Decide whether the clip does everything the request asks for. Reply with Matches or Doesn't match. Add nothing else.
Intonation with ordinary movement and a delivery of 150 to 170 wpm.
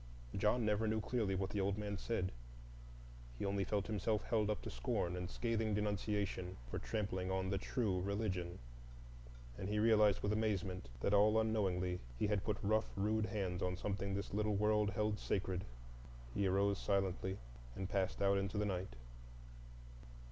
Doesn't match